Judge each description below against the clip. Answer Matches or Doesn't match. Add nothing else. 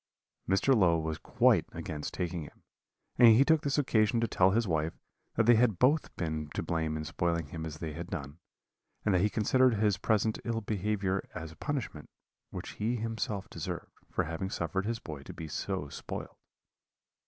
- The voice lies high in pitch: Doesn't match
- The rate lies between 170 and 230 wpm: Matches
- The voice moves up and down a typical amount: Doesn't match